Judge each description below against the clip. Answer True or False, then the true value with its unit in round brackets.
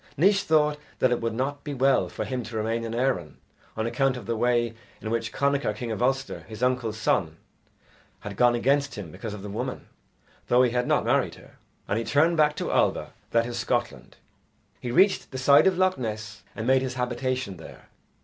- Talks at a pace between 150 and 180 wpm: False (205 wpm)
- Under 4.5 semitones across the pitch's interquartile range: True (3.3 semitones)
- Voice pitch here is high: False (125 Hz)